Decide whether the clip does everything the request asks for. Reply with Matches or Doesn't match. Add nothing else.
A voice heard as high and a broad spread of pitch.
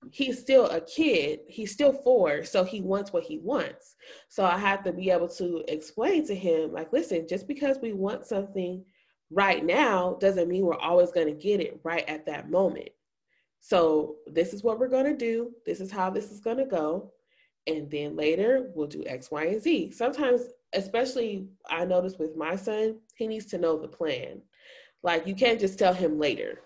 Matches